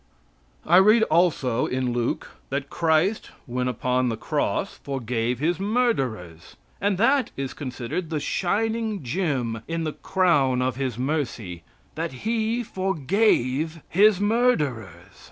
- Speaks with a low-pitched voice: No, medium, 150 Hz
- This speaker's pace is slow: Yes, slow, 125 wpm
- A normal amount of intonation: No, wide, 7.5 semitones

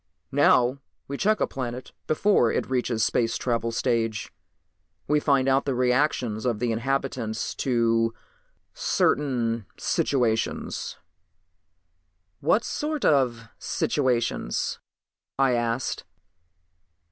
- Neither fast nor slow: No, slow, 100 wpm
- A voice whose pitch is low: Yes, low, 125 Hz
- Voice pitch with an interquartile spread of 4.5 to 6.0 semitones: No, average, 2.9 semitones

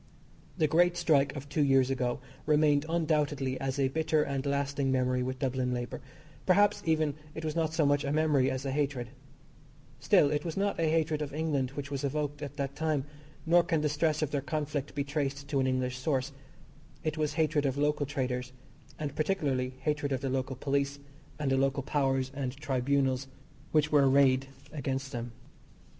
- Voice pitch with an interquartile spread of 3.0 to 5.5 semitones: No, narrow, 2.4 semitones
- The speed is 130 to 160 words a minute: No, average, 185 wpm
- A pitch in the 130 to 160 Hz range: Yes, medium, 140 Hz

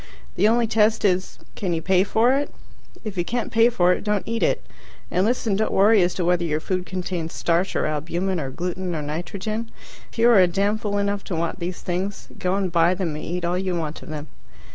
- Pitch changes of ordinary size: Yes, average, 3.3 semitones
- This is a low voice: No, medium, 185 Hz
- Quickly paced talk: Yes, fast, 230 wpm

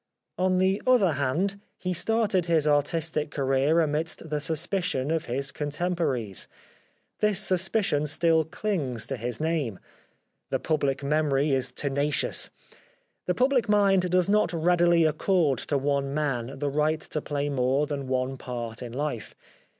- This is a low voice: No, medium, 150 Hz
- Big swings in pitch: No, average, 4.5 semitones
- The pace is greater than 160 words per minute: No, average, 145 wpm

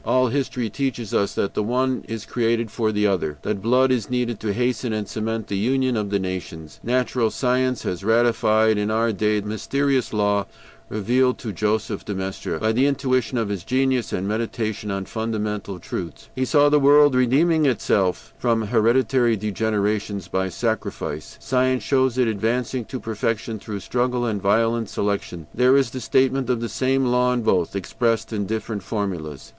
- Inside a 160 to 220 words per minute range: Yes, average, 180 wpm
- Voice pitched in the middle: No, low, 115 Hz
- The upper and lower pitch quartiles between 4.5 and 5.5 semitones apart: No, average, 3.4 semitones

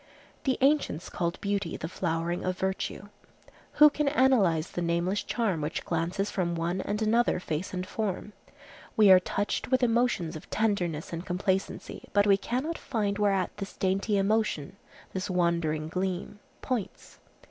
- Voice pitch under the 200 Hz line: Yes, high, 190 Hz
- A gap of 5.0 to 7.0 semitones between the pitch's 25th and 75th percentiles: No, average, 3.8 semitones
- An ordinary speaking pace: Yes, average, 150 wpm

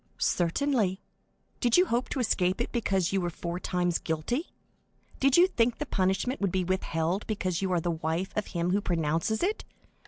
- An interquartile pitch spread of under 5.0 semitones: No, wide, 5.4 semitones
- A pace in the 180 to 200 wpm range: Yes, average, 185 wpm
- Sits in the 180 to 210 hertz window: Yes, high, 190 Hz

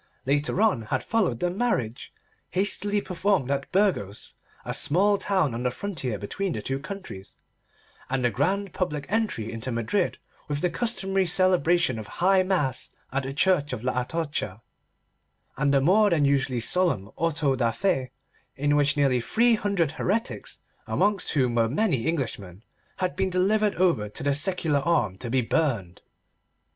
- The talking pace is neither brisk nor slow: Yes, average, 160 wpm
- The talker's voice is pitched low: No, medium, 150 Hz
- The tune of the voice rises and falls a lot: Yes, wide, 7.0 semitones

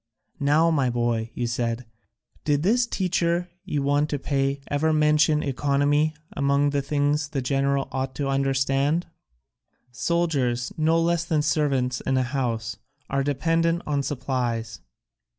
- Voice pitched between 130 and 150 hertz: Yes, medium, 140 Hz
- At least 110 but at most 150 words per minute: Yes, slow, 135 wpm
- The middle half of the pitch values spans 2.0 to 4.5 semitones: Yes, average, 2.7 semitones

